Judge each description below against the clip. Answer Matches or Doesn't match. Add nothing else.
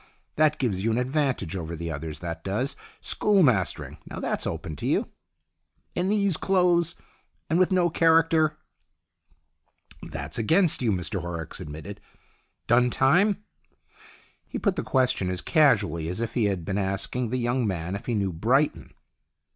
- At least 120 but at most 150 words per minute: Doesn't match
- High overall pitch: Doesn't match